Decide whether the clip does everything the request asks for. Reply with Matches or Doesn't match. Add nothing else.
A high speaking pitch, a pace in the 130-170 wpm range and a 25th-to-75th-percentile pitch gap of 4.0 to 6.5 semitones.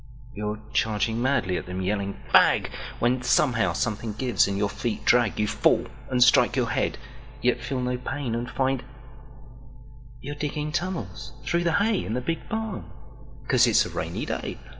Doesn't match